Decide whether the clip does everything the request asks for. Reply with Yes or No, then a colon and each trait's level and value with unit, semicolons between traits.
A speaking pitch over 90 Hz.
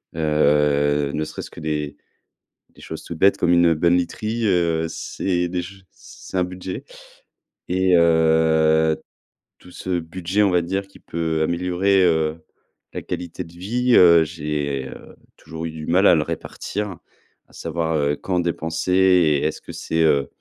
No: very low, 85 Hz